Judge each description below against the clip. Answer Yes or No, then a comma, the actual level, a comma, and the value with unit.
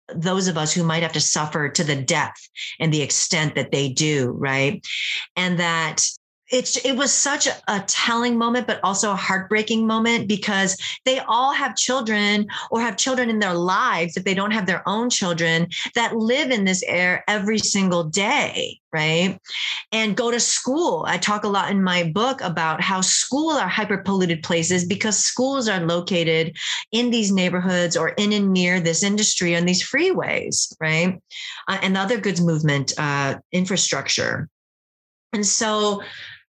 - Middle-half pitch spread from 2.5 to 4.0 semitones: No, average, 4.5 semitones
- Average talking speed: Yes, average, 170 wpm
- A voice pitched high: Yes, high, 195 Hz